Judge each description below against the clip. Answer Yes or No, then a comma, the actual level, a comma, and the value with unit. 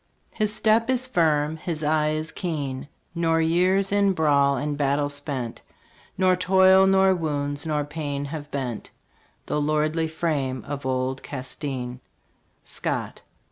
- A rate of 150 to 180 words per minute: No, slow, 135 wpm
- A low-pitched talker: No, medium, 155 Hz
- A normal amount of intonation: Yes, average, 3.8 semitones